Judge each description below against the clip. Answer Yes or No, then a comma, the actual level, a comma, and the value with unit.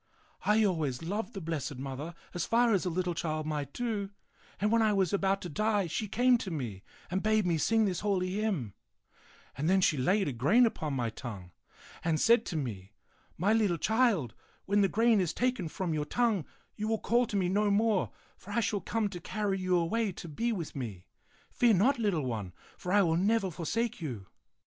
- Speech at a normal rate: No, fast, 210 wpm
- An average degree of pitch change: No, wide, 5.7 semitones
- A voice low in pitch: No, high, 190 Hz